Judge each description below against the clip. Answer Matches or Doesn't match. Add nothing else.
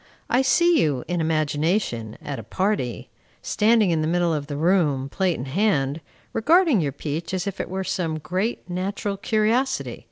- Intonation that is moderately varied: Doesn't match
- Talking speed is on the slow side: Doesn't match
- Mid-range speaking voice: Matches